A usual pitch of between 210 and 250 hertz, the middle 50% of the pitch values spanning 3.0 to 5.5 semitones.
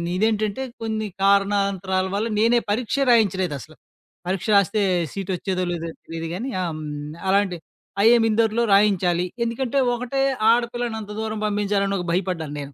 No: high, 200 Hz; average, 3.3 semitones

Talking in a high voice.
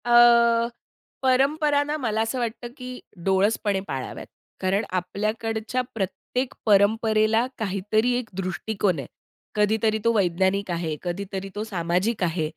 Yes: high, 215 Hz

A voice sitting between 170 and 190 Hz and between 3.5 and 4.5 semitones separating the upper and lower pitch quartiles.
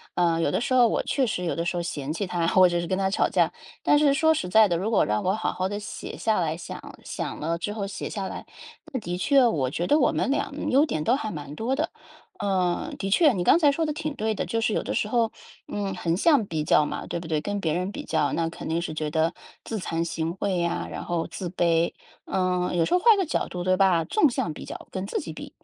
No: medium, 185 Hz; average, 5.3 semitones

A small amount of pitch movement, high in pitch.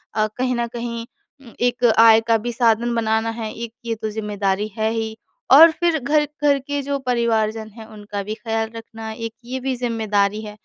Yes: narrow, 2.1 semitones; high, 225 Hz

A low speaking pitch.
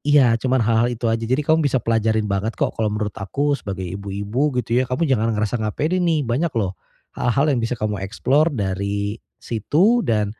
Yes: low, 115 Hz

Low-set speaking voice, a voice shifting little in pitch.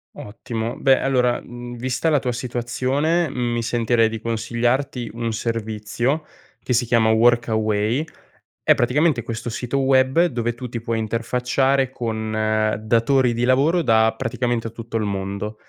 Yes: low, 120 Hz; narrow, 2.3 semitones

